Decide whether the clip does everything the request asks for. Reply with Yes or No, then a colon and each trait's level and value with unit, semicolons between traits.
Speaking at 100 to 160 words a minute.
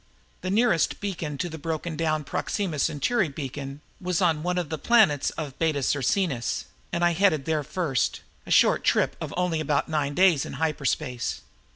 No: average, 175 wpm